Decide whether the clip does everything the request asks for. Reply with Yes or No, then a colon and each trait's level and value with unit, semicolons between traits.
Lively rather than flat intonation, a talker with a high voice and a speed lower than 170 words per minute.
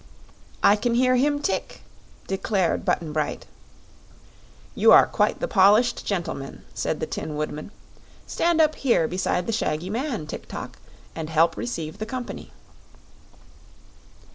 Yes: wide, 7.4 semitones; high, 200 Hz; slow, 135 wpm